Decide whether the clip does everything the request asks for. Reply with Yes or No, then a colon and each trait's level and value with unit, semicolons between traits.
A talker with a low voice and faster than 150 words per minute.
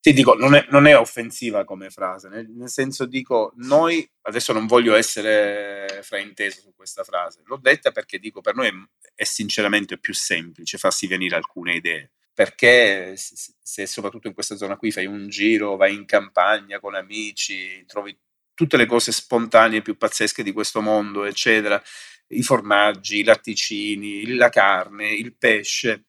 Yes: low, 105 Hz; fast, 170 wpm